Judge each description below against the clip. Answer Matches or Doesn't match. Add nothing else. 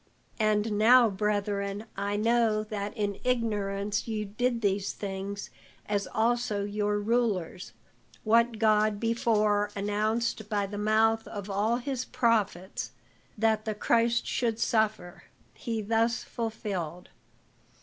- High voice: Matches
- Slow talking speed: Matches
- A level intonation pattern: Matches